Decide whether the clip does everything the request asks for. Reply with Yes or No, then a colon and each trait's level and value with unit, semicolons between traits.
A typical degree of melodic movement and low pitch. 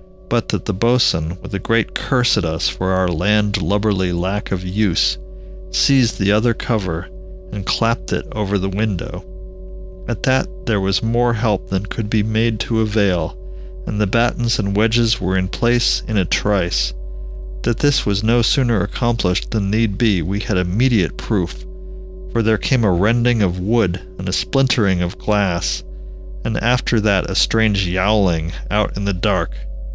Yes: average, 3.7 semitones; low, 105 Hz